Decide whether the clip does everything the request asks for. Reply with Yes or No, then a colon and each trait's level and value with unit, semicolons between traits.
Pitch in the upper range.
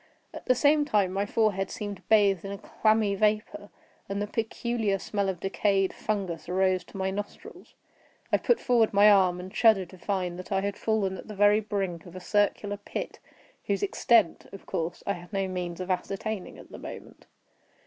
Yes: high, 200 Hz